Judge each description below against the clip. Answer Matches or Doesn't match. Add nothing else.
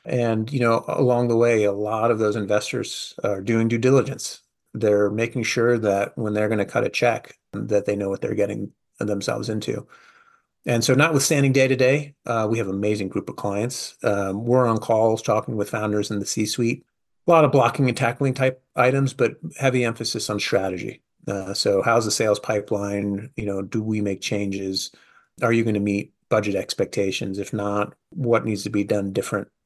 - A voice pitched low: Matches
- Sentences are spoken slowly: Doesn't match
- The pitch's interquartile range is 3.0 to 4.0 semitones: Matches